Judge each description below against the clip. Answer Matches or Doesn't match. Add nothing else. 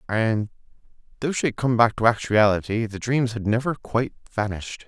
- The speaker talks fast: Doesn't match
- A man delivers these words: Matches